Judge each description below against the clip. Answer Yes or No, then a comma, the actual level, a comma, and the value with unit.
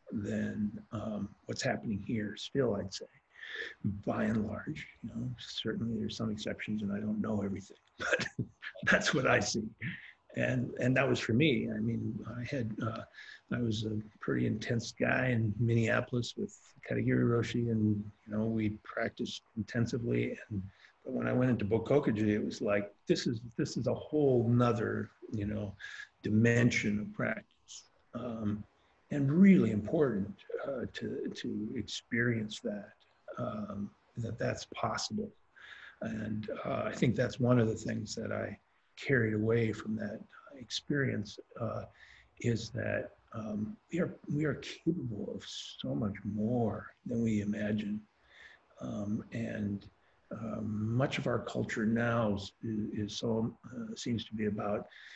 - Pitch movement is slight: Yes, narrow, 2.0 semitones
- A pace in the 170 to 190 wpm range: No, average, 150 wpm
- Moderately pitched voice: No, low, 110 Hz